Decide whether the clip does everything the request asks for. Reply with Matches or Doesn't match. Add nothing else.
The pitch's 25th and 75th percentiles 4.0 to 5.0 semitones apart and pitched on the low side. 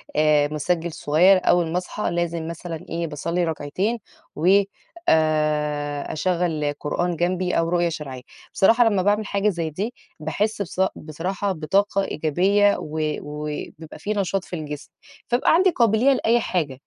Doesn't match